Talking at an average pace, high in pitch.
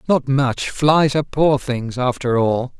No: average, 170 wpm; low, 135 Hz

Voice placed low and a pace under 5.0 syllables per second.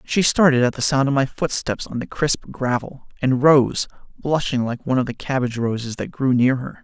No: low, 130 Hz; 5.3 syllables/s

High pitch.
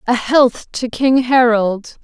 Yes: high, 240 Hz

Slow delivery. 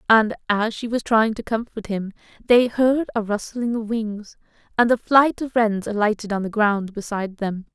No: average, 195 wpm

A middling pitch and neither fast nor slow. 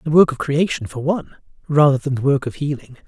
No: medium, 145 Hz; fast, 235 wpm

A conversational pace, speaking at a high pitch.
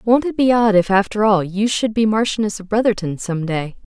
No: fast, 230 wpm; high, 210 Hz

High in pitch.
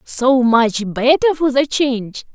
Yes: very high, 255 Hz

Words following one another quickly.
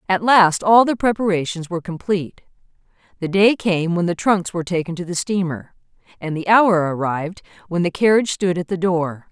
No: average, 185 wpm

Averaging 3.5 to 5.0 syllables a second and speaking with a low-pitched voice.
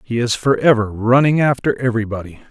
No: 6.0 syllables/s; low, 120 Hz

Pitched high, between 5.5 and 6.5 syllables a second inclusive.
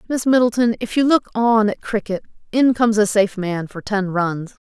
No: high, 215 Hz; 5.2 syllables/s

